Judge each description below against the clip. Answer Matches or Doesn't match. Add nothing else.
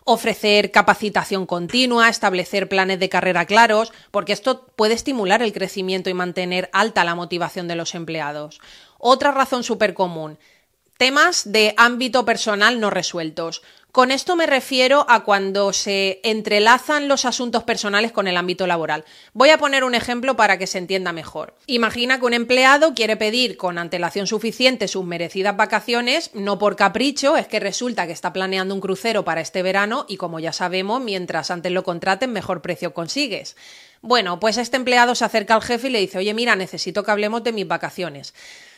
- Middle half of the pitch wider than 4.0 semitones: Matches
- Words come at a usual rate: Matches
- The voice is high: Matches